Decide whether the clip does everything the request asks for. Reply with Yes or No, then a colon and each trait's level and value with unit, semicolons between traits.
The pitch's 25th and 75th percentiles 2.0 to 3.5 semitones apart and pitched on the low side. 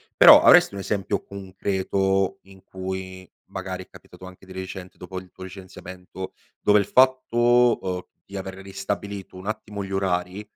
No: narrow, 1.3 semitones; very low, 95 Hz